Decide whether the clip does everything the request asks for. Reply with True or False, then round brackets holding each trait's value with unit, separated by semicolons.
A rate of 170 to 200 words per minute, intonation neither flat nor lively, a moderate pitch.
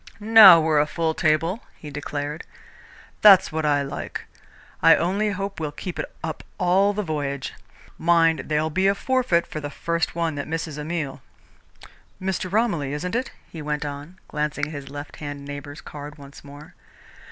True (175 wpm; 3.8 semitones; 155 Hz)